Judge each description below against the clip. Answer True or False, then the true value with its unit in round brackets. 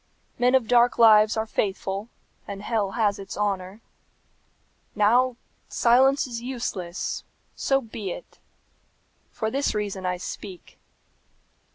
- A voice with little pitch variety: False (3.5 semitones)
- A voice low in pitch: False (215 Hz)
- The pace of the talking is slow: True (115 wpm)